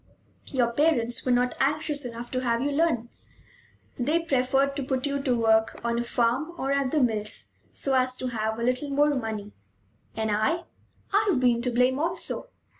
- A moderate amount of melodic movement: Yes, average, 3.3 semitones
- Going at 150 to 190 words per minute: Yes, average, 185 wpm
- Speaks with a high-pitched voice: Yes, very high, 255 Hz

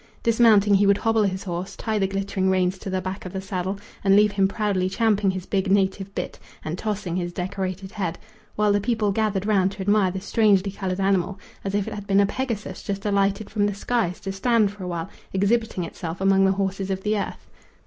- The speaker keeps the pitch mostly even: Yes, narrow, 1.6 semitones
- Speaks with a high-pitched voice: Yes, high, 195 Hz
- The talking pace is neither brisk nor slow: No, fast, 220 wpm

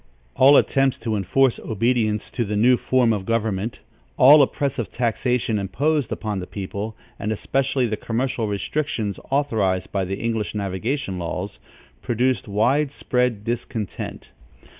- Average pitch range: Yes, average, 4.0 semitones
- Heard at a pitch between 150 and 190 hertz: No, low, 115 Hz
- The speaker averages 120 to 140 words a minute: Yes, slow, 135 wpm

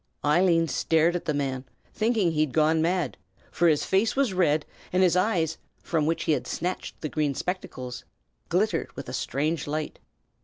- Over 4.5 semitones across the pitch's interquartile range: No, average, 3.3 semitones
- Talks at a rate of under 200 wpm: Yes, average, 180 wpm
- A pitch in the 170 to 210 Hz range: No, medium, 160 Hz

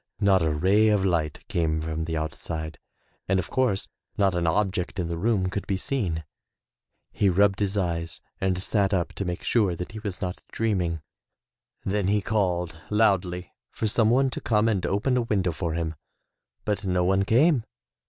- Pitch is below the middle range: Yes, very low, 95 Hz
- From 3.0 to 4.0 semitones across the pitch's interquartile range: Yes, average, 3.5 semitones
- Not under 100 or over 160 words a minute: No, average, 185 wpm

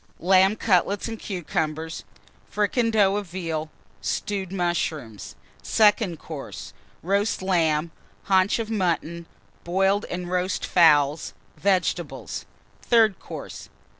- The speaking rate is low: Yes, slow, 100 wpm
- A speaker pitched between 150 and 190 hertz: Yes, medium, 185 Hz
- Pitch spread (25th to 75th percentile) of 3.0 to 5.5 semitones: Yes, average, 3.5 semitones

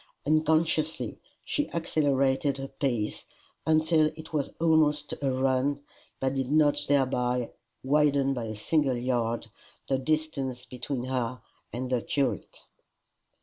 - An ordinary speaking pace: No, slow, 120 wpm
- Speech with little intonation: No, average, 3.2 semitones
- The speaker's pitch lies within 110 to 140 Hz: Yes, low, 135 Hz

